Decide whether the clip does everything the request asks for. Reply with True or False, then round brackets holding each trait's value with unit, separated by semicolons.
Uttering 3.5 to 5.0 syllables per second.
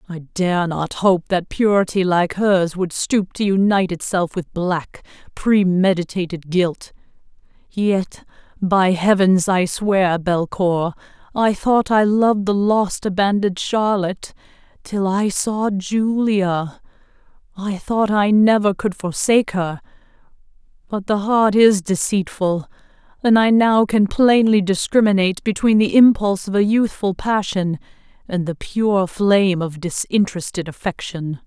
True (4.1 syllables/s)